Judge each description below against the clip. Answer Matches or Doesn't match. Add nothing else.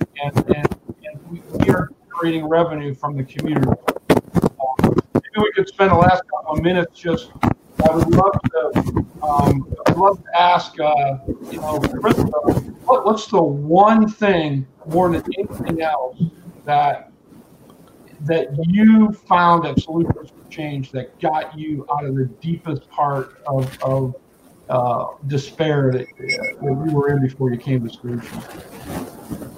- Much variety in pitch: Doesn't match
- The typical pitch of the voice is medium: Matches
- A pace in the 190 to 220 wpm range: Doesn't match